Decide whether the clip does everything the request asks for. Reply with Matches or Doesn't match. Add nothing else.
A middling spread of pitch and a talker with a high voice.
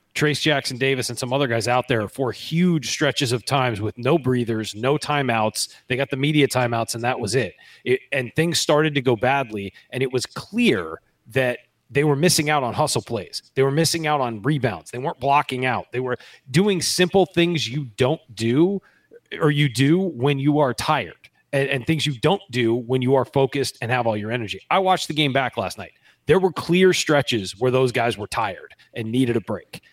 Doesn't match